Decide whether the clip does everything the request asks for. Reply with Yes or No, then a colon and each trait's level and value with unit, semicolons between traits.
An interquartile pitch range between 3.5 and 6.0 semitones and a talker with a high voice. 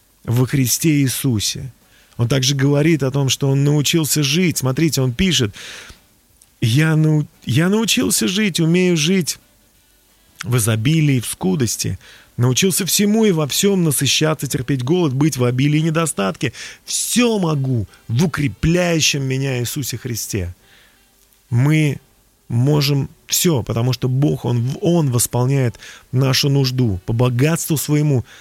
No: average, 4.5 semitones; medium, 140 Hz